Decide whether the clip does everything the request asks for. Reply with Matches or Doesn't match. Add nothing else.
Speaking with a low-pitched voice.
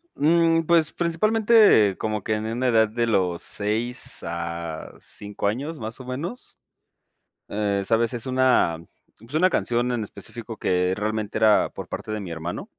Matches